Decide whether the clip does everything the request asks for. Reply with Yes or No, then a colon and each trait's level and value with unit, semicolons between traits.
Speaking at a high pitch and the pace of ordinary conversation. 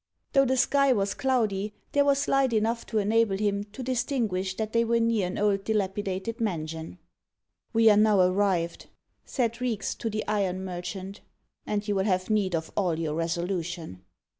Yes: high, 205 Hz; average, 170 wpm